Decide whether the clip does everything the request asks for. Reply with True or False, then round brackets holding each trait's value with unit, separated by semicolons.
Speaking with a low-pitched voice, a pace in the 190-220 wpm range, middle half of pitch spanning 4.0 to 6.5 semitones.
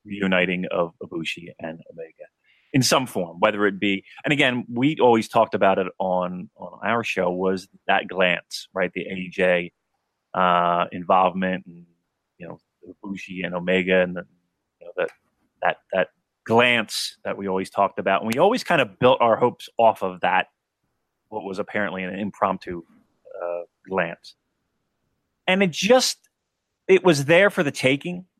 False (95 Hz; 160 wpm; 5.3 semitones)